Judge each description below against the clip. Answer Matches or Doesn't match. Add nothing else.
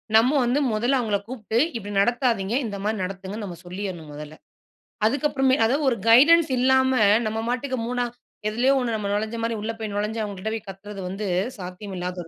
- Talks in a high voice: Matches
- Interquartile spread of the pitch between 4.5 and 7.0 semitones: Doesn't match